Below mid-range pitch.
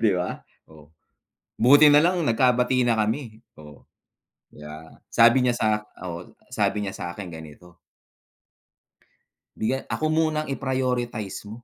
Yes: low, 115 Hz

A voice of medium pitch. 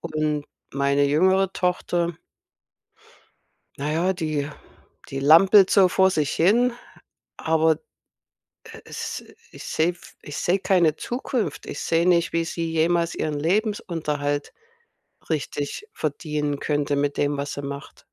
Yes: medium, 160 Hz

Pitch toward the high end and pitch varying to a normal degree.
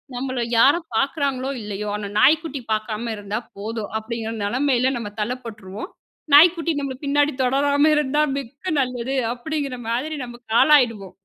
Yes: very high, 255 Hz; average, 4.3 semitones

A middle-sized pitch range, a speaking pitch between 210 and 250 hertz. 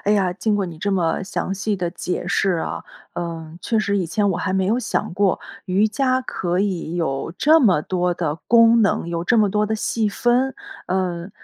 No: average, 3.6 semitones; high, 190 Hz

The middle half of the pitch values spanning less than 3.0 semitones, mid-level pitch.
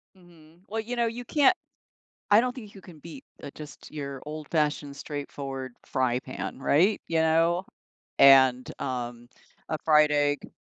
No: average, 4.4 semitones; medium, 150 Hz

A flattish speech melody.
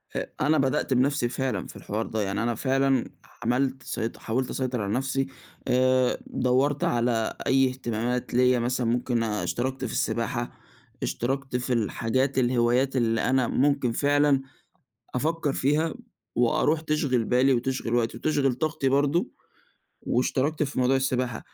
Yes: narrow, 2.2 semitones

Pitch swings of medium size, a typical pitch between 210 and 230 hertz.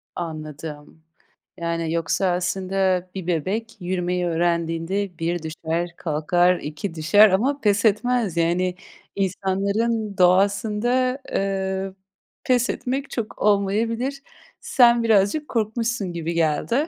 No: average, 4.5 semitones; high, 190 Hz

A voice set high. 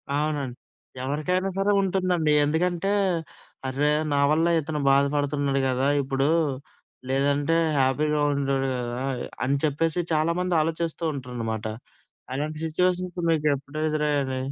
No: medium, 150 Hz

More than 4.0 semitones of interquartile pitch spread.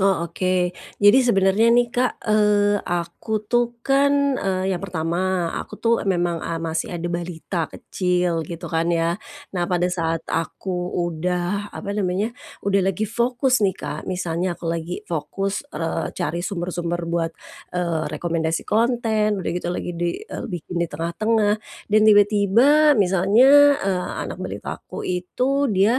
No: average, 3.4 semitones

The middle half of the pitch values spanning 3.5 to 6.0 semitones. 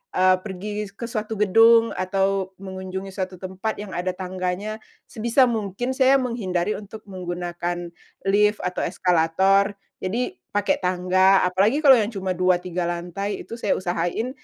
No: average, 2.7 semitones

